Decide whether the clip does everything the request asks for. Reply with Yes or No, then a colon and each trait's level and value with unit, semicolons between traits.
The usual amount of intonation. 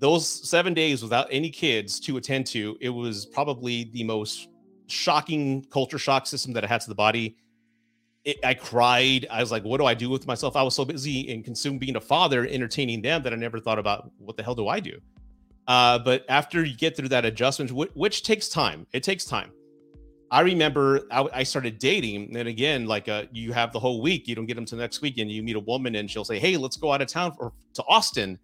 Yes: average, 3.7 semitones